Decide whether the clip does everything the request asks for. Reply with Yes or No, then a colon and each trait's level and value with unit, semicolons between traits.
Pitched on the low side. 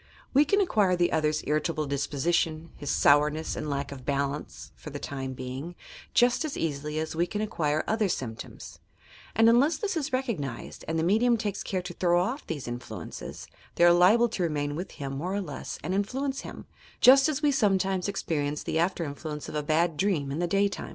No: medium, 170 Hz